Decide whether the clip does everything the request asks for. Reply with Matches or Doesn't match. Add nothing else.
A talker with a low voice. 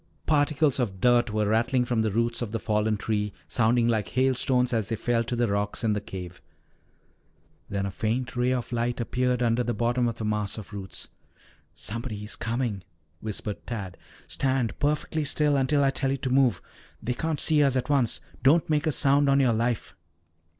Matches